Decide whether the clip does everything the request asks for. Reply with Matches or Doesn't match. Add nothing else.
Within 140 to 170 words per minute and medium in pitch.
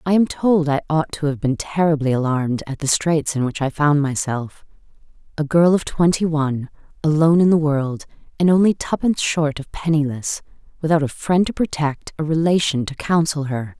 Doesn't match